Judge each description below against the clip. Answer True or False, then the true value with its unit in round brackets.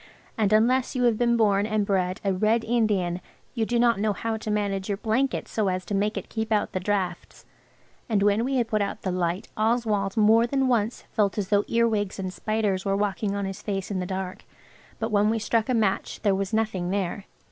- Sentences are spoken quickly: True (225 wpm)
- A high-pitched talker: True (210 Hz)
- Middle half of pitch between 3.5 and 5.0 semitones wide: False (2.4 semitones)